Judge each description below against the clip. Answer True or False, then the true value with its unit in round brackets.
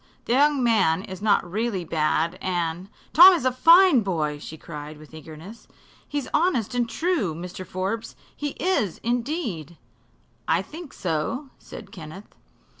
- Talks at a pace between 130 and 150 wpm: True (145 wpm)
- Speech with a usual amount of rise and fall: False (7.9 semitones)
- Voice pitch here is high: True (200 Hz)